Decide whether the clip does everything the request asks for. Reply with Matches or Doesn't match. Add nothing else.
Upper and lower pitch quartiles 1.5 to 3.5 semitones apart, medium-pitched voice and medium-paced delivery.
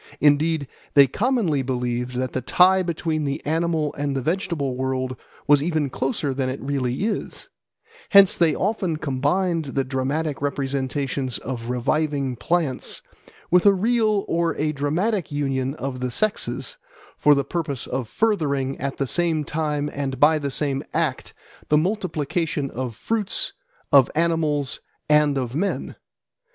Doesn't match